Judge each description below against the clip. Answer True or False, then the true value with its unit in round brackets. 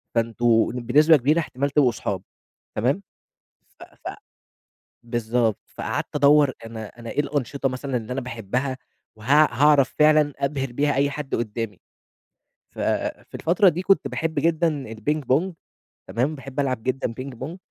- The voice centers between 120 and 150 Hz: True (135 Hz)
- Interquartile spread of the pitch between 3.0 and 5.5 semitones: True (4.0 semitones)